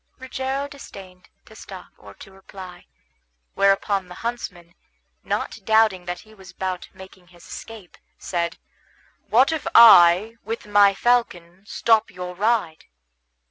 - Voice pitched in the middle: No, high, 195 Hz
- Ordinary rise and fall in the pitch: Yes, average, 3.9 semitones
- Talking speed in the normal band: No, slow, 130 wpm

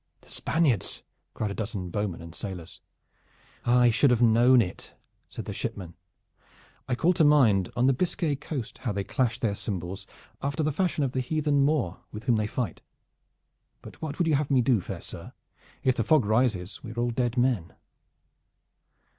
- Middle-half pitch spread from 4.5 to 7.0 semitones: Yes, average, 5.1 semitones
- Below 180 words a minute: No, average, 185 wpm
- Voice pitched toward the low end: Yes, low, 120 Hz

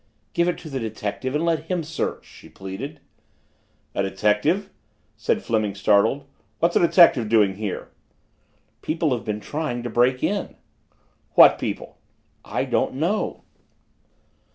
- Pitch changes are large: Yes, wide, 7.5 semitones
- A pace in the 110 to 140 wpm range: Yes, slow, 135 wpm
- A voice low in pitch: Yes, low, 130 Hz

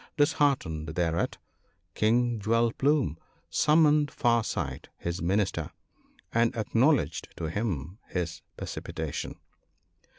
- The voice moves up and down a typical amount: No, wide, 6.6 semitones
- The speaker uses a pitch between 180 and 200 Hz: No, low, 105 Hz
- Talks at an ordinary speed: No, slow, 100 wpm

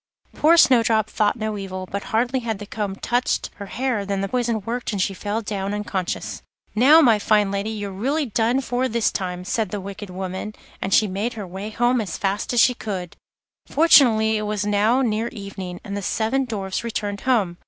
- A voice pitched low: No, high, 215 Hz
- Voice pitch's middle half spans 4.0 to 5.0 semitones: No, average, 3.1 semitones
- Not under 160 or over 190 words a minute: No, average, 200 wpm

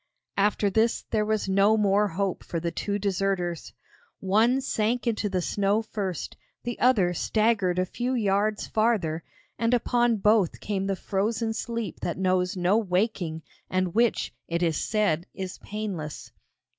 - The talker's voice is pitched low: No, high, 200 Hz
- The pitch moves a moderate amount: Yes, average, 3.1 semitones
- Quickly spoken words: No, average, 150 wpm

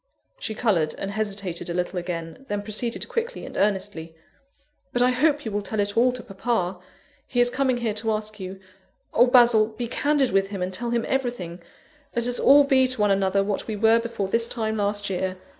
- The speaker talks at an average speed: No, fast, 210 wpm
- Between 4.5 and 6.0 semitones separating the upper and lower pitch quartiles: No, average, 3.8 semitones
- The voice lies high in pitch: Yes, high, 215 Hz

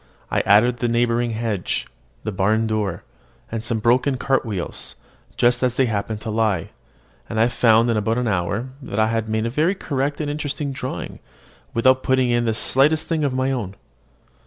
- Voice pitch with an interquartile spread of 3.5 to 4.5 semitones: No, average, 3.1 semitones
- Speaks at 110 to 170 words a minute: No, average, 185 wpm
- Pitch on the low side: Yes, low, 115 Hz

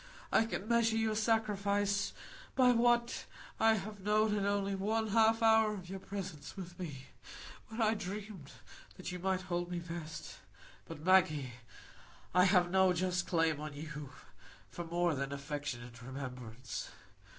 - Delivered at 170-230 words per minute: No, average, 150 wpm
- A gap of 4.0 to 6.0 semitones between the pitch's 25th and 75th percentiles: Yes, average, 5.3 semitones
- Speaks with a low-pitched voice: No, medium, 185 Hz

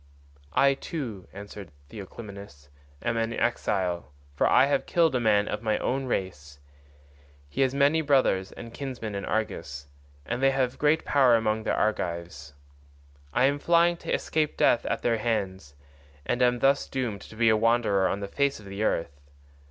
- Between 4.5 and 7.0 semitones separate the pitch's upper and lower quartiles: Yes, wide, 5.5 semitones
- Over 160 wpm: Yes, average, 170 wpm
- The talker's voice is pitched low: Yes, low, 115 Hz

